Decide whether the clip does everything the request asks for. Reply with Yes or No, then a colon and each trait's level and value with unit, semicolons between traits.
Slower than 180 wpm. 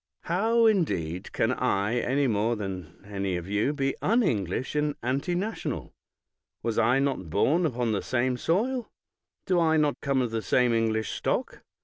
Yes: average, 155 wpm